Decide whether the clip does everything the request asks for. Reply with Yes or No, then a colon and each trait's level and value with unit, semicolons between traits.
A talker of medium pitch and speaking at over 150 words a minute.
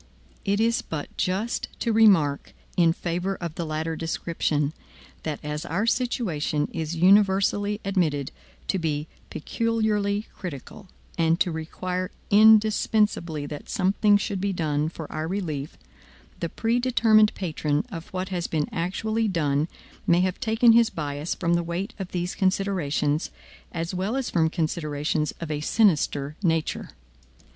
No: medium, 175 Hz; average, 140 wpm